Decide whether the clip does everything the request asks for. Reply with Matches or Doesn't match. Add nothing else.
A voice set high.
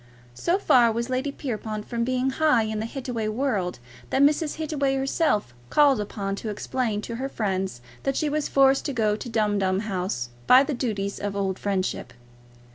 Matches